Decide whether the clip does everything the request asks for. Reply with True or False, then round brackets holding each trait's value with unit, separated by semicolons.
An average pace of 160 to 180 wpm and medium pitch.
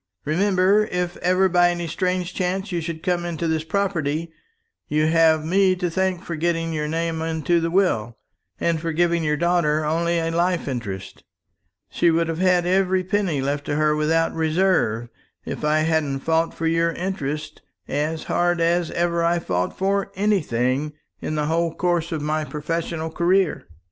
True (170 wpm; 165 Hz)